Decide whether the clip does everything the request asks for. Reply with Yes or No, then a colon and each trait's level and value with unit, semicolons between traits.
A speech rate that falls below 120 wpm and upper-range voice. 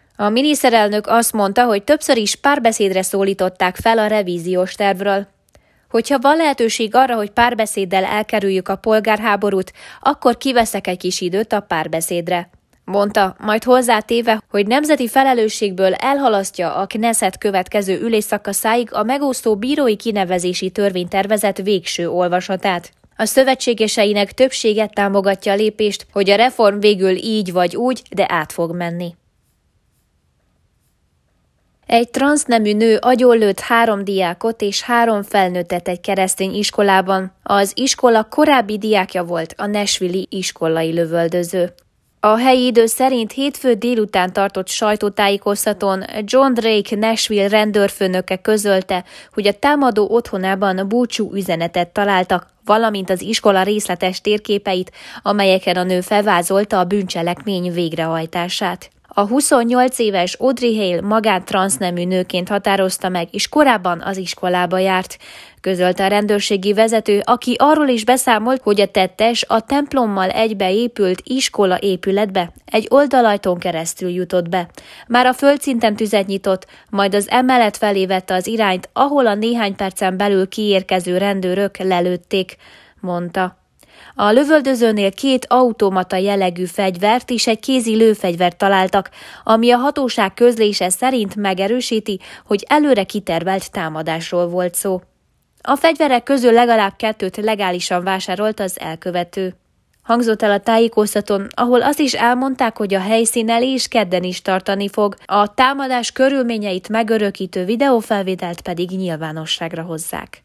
No: average, 125 wpm; high, 205 Hz